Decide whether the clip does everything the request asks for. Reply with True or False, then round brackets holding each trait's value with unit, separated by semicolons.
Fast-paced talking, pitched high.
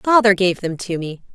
True (225 wpm; 195 Hz)